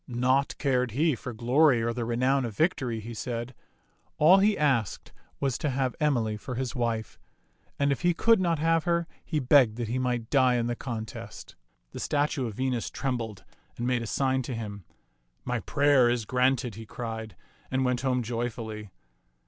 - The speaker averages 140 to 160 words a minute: No, average, 185 wpm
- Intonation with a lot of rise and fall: No, average, 3.1 semitones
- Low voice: Yes, low, 125 Hz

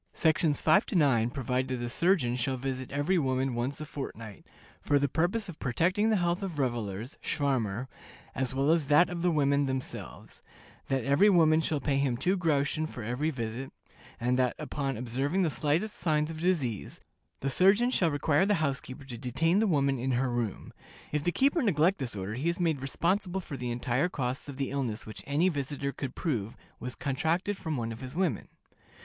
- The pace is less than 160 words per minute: No, average, 195 wpm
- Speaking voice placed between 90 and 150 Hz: Yes, medium, 140 Hz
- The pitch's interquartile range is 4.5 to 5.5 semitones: Yes, average, 4.9 semitones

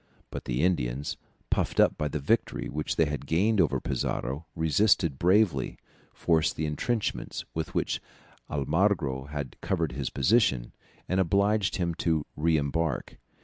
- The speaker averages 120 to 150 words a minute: Yes, average, 145 wpm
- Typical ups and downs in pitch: Yes, average, 4.3 semitones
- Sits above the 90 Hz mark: No, very low, 80 Hz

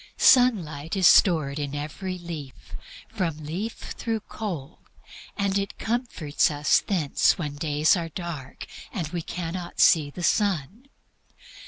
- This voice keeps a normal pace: No, slow, 130 wpm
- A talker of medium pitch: Yes, medium, 170 Hz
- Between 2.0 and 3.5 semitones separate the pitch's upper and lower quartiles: No, average, 4.9 semitones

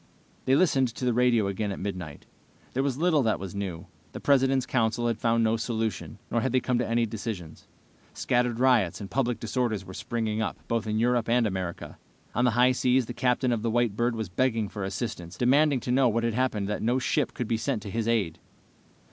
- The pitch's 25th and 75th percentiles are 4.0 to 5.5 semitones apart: No, average, 2.7 semitones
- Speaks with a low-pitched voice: Yes, low, 115 Hz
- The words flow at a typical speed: No, fast, 220 wpm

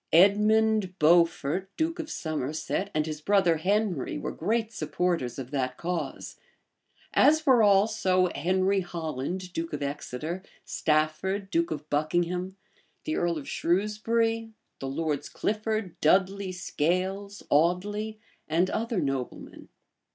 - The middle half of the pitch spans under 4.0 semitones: No, average, 4.8 semitones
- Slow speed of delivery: Yes, slow, 120 wpm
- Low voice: No, medium, 180 Hz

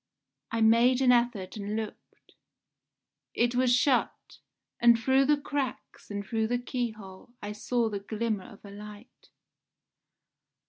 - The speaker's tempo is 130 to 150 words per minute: Yes, slow, 135 wpm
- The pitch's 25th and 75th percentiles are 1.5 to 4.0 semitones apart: Yes, average, 2.9 semitones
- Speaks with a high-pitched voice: Yes, high, 230 Hz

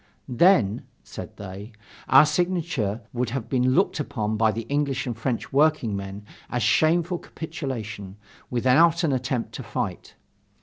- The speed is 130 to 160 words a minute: Yes, average, 140 wpm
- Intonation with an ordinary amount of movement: No, wide, 5.9 semitones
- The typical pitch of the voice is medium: No, low, 125 Hz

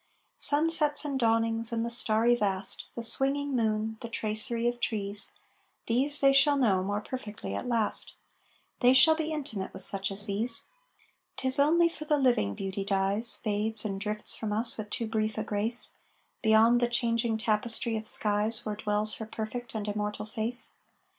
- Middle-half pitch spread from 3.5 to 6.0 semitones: No, narrow, 2.6 semitones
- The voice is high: Yes, high, 225 Hz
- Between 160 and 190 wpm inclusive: Yes, average, 170 wpm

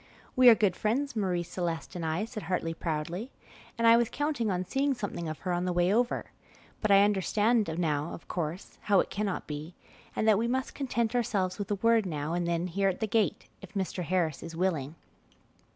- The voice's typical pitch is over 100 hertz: Yes, high, 190 Hz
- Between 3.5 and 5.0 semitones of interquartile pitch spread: Yes, average, 4.5 semitones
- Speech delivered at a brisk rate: Yes, fast, 210 wpm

